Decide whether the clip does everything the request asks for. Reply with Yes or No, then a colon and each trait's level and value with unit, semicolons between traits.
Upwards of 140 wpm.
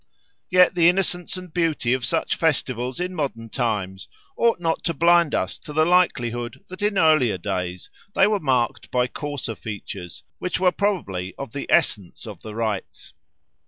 Yes: average, 165 wpm